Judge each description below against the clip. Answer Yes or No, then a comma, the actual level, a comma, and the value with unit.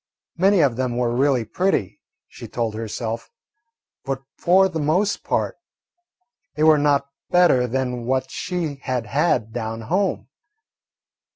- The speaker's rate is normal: No, slow, 130 wpm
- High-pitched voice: No, low, 135 Hz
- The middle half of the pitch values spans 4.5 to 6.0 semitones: Yes, average, 5.3 semitones